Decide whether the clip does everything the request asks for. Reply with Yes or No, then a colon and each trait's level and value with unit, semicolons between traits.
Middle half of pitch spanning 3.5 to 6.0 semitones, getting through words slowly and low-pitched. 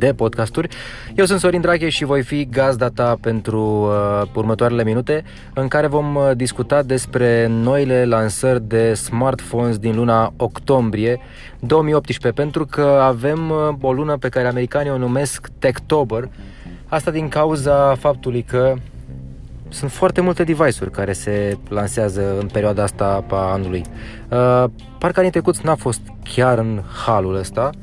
No: average, 4.5 semitones; average, 145 wpm; low, 125 Hz